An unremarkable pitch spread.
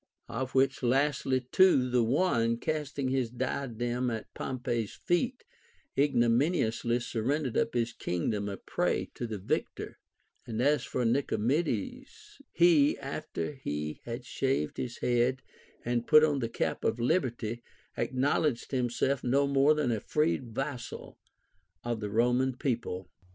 Yes: average, 3.3 semitones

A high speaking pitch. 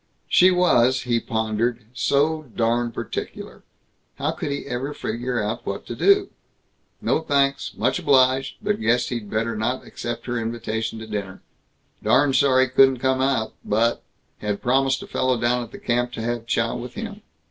No: low, 125 Hz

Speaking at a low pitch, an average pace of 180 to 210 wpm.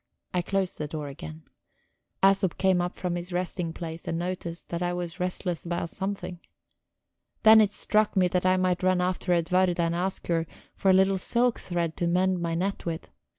No: medium, 180 Hz; average, 195 wpm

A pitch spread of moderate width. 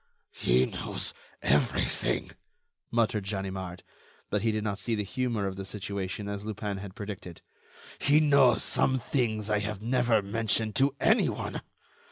Yes: average, 3.0 semitones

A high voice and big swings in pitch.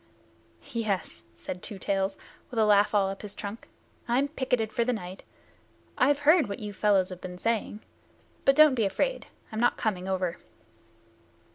No: high, 210 Hz; average, 3.9 semitones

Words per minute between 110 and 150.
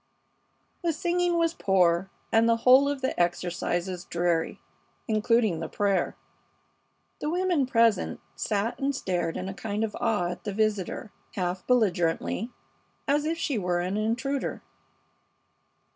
Yes: average, 140 wpm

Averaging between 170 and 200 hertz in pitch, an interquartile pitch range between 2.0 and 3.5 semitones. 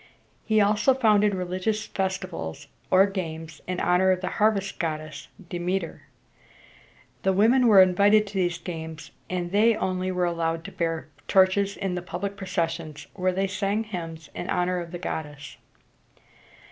Yes: medium, 185 Hz; average, 3.0 semitones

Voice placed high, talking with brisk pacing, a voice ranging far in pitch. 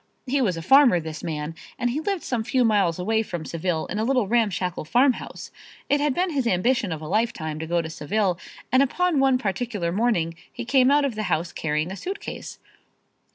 Yes: high, 215 Hz; fast, 210 wpm; wide, 7.2 semitones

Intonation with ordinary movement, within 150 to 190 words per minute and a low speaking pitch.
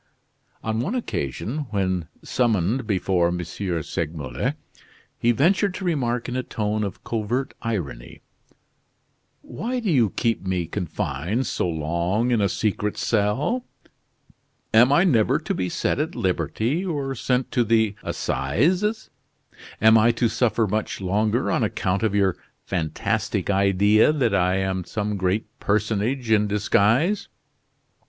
No: average, 4.8 semitones; slow, 135 wpm; low, 110 Hz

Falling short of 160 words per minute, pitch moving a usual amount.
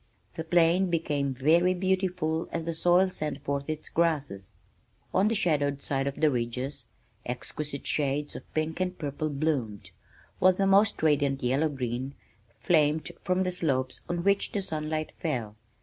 Yes: average, 150 wpm; average, 4.0 semitones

